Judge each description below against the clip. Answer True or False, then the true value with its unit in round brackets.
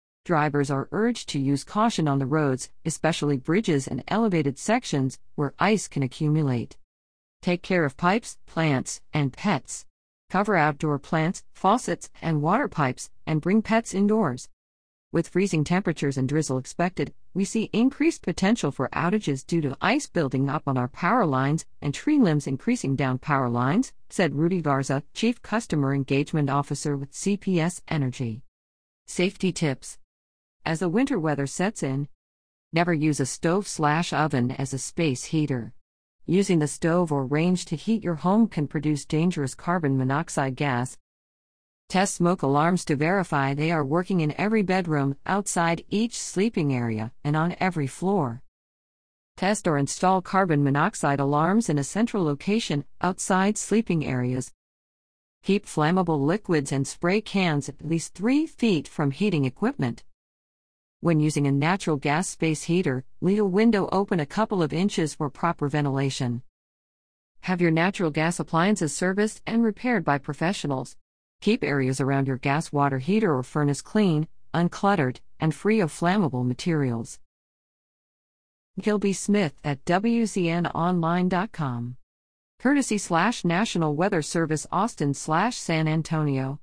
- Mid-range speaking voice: True (155 Hz)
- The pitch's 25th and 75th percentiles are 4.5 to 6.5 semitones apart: True (5.4 semitones)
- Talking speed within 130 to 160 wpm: True (140 wpm)